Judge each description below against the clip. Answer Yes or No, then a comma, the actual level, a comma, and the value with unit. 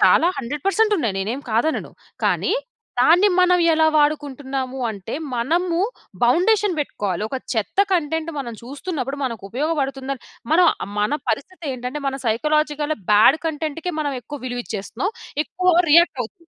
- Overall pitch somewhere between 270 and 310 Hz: Yes, very high, 290 Hz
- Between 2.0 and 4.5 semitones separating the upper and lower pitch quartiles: No, average, 5.1 semitones